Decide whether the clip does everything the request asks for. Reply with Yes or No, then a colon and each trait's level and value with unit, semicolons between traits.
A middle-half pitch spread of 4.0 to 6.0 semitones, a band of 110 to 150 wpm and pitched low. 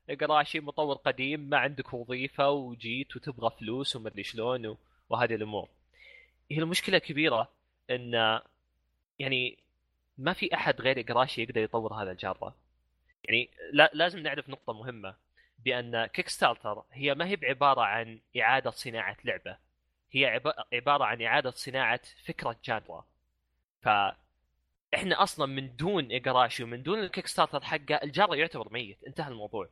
Yes: average, 5.0 semitones; average, 130 wpm; low, 125 Hz